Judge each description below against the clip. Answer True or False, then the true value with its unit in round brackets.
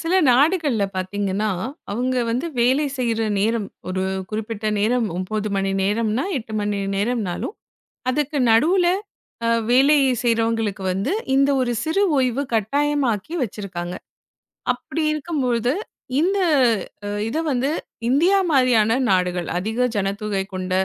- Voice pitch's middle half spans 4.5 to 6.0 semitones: True (5.2 semitones)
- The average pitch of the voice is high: True (230 Hz)